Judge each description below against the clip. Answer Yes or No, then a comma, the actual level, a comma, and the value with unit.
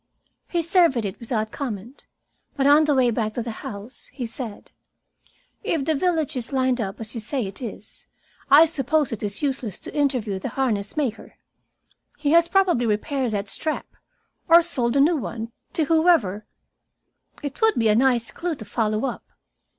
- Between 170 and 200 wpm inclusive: Yes, average, 175 wpm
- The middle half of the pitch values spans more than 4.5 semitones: Yes, wide, 5.5 semitones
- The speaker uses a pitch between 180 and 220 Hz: No, very high, 255 Hz